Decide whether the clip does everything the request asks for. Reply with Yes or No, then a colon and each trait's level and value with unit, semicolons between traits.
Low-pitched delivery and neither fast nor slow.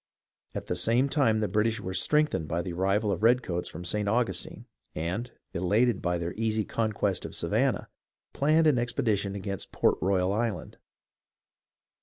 Yes: low, 105 Hz; average, 160 wpm